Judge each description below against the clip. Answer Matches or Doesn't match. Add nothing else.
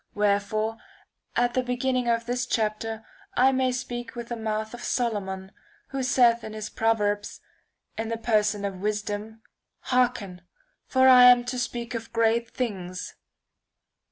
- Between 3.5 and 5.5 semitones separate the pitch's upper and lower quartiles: Doesn't match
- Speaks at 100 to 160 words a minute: Matches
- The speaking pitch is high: Matches